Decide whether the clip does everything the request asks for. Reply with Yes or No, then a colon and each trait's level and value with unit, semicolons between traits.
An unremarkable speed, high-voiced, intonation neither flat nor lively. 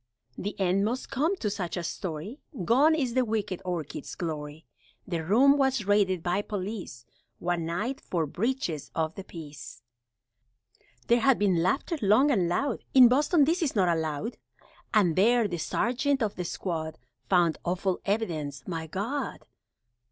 No: average, 155 wpm; high, 195 Hz; wide, 6.4 semitones